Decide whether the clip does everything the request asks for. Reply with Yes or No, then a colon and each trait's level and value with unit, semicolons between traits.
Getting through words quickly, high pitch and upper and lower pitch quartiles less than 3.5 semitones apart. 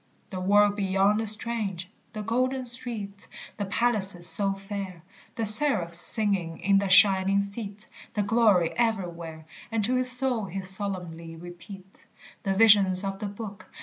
No: average, 150 wpm; high, 200 Hz; average, 2.7 semitones